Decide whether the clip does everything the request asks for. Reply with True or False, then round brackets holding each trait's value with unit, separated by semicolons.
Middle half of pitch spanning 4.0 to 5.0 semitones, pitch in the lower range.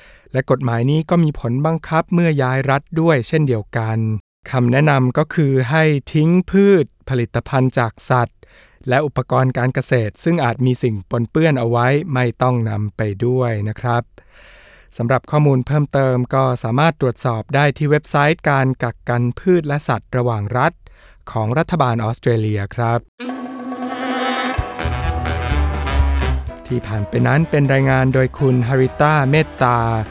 True (4.3 semitones; 130 Hz)